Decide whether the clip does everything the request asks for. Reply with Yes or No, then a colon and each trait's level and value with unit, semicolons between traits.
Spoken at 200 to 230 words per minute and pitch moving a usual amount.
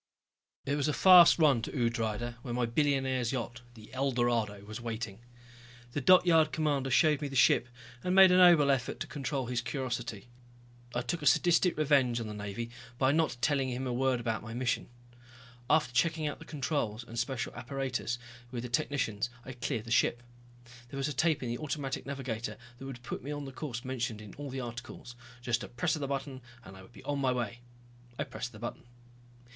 Yes: fast, 205 wpm; average, 3.3 semitones